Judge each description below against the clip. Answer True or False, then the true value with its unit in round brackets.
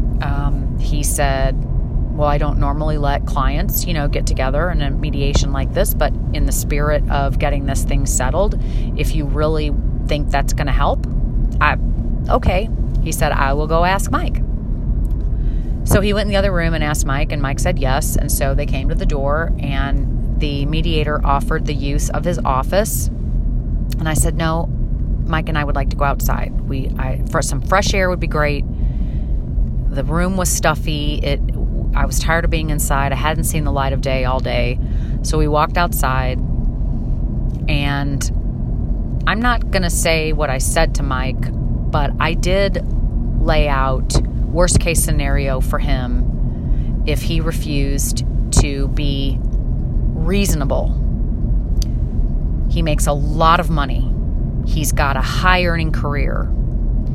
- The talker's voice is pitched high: False (140 Hz)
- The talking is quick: False (165 wpm)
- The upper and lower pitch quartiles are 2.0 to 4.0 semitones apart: False (4.4 semitones)